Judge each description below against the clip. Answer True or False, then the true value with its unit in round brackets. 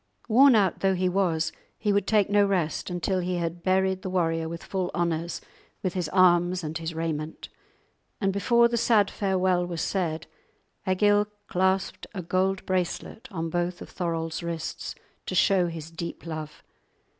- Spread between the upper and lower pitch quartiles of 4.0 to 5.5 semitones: False (2.6 semitones)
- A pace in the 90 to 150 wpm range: False (165 wpm)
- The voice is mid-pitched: True (180 Hz)